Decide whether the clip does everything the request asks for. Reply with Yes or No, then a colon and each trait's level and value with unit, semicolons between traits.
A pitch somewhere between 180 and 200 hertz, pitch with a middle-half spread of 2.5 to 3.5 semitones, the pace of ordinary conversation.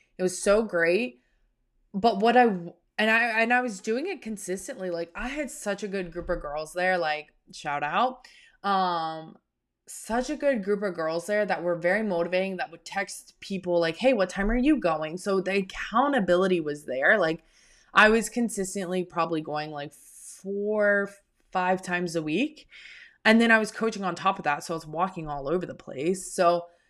No: high, 190 Hz; average, 4.4 semitones; average, 190 wpm